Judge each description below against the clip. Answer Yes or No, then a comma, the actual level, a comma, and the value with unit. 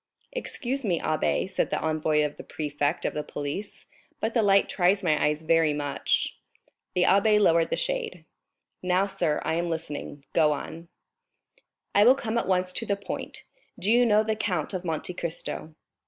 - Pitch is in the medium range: Yes, medium, 175 Hz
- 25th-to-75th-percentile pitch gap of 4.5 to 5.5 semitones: Yes, average, 5.2 semitones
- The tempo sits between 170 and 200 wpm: Yes, average, 175 wpm